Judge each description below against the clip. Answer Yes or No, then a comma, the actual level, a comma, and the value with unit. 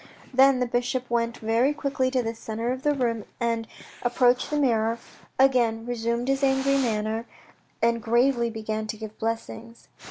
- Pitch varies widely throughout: No, narrow, 2.4 semitones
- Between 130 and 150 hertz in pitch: No, high, 235 Hz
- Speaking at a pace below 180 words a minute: Yes, average, 165 wpm